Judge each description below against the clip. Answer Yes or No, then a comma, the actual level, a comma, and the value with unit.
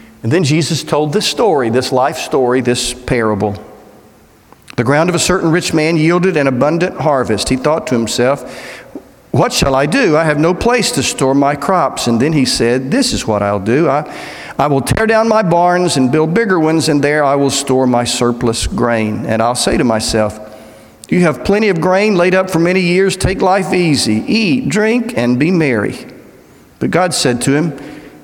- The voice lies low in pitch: No, medium, 145 Hz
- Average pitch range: No, wide, 6.8 semitones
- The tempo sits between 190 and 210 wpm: Yes, average, 200 wpm